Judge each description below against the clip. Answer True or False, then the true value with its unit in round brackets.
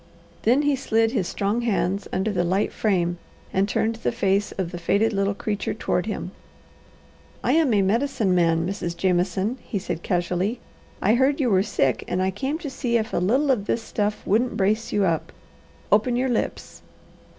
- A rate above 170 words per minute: True (185 wpm)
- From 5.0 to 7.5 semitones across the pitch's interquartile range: False (4.0 semitones)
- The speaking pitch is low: False (205 Hz)